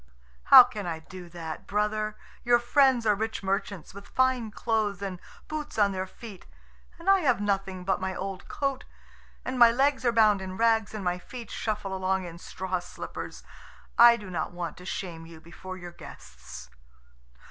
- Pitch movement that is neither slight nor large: Yes, average, 4.0 semitones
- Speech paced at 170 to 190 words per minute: Yes, average, 180 wpm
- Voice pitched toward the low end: No, high, 200 Hz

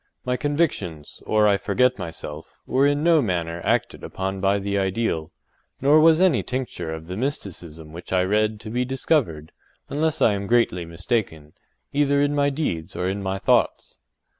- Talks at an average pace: Yes, average, 170 wpm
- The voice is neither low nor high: No, low, 100 Hz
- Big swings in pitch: Yes, wide, 7.8 semitones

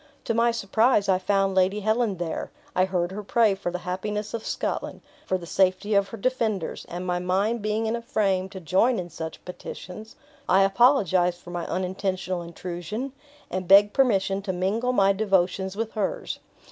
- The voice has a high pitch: Yes, high, 195 Hz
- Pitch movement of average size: Yes, average, 3.0 semitones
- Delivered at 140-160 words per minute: No, average, 180 wpm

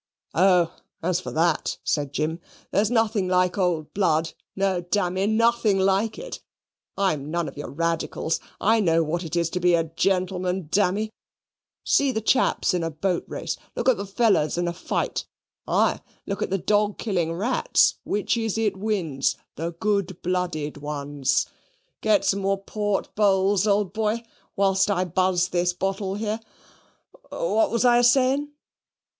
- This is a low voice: No, high, 190 Hz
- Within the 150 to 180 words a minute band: Yes, average, 160 wpm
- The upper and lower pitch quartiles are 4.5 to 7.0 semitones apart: No, average, 3.6 semitones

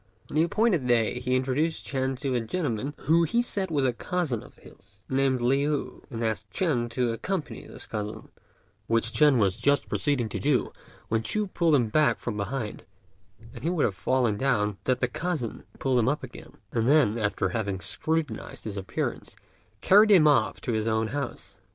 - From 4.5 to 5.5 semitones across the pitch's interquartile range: Yes, average, 5.2 semitones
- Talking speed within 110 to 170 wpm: No, average, 190 wpm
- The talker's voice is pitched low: Yes, low, 130 Hz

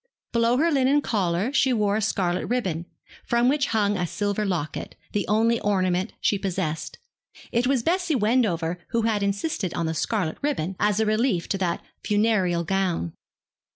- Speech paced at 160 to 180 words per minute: Yes, average, 165 wpm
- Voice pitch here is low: No, high, 205 Hz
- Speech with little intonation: No, average, 4.5 semitones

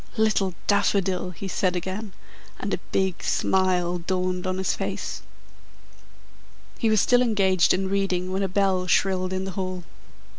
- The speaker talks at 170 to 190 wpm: No, average, 150 wpm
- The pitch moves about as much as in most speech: No, narrow, 1.2 semitones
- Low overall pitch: No, high, 190 Hz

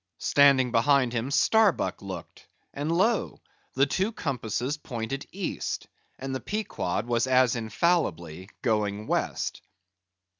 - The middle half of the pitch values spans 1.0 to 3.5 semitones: No, average, 4.8 semitones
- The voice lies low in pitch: Yes, low, 130 Hz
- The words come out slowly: Yes, slow, 115 wpm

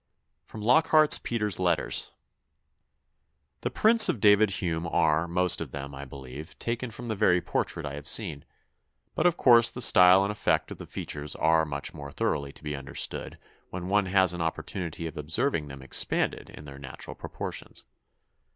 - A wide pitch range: Yes, wide, 6.4 semitones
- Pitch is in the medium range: No, very low, 90 Hz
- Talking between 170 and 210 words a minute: Yes, average, 175 wpm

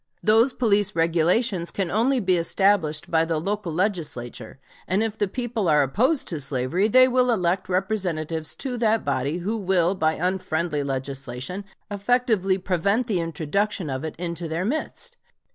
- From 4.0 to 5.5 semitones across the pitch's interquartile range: Yes, average, 5.1 semitones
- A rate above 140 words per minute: Yes, average, 155 wpm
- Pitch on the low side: No, medium, 185 Hz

